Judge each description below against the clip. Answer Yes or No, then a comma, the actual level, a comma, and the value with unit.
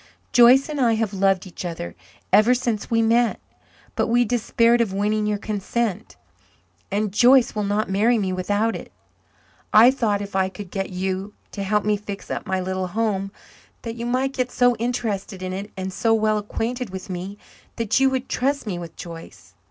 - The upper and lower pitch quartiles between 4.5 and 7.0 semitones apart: No, average, 3.5 semitones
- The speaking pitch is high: Yes, high, 210 Hz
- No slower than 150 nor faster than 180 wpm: No, average, 190 wpm